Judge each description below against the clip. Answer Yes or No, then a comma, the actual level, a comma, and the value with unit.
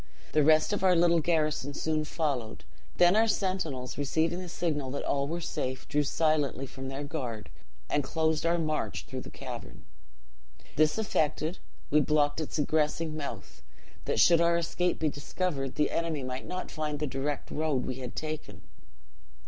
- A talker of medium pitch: Yes, medium, 155 Hz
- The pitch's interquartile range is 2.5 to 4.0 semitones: Yes, average, 3.0 semitones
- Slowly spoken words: No, average, 170 wpm